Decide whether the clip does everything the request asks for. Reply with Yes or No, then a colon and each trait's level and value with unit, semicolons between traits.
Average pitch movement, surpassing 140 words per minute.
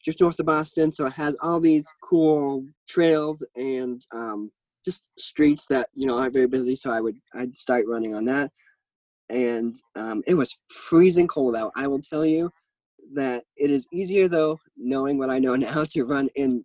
Yes: average, 3.8 semitones; average, 190 wpm